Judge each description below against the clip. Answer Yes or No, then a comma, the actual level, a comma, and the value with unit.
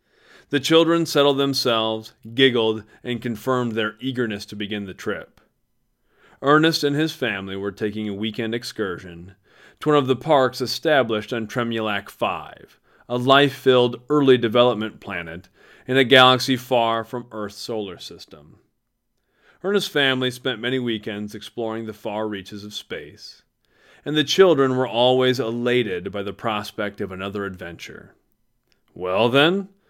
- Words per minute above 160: No, average, 140 wpm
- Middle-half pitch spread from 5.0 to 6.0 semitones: No, average, 3.8 semitones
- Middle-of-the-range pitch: No, low, 120 Hz